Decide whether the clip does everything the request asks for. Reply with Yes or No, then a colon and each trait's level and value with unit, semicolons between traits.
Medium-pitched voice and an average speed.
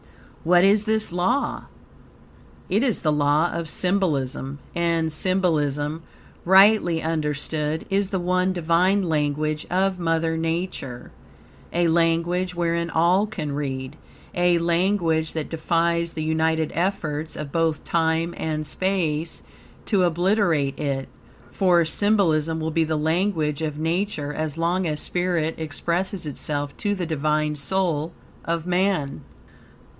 No: medium, 165 Hz; slow, 125 wpm